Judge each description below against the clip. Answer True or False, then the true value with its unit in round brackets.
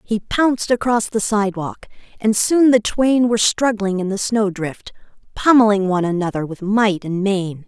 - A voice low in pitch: False (210 Hz)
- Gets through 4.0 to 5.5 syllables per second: True (4.8 syllables/s)